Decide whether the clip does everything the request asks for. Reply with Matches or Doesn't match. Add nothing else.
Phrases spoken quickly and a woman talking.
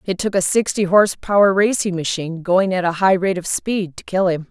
Matches